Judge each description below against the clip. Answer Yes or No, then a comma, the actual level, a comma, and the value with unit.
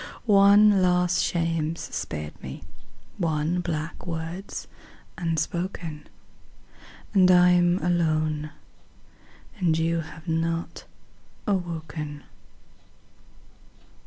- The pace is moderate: No, slow, 75 wpm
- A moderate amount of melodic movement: No, narrow, 2.1 semitones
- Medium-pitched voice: Yes, medium, 170 Hz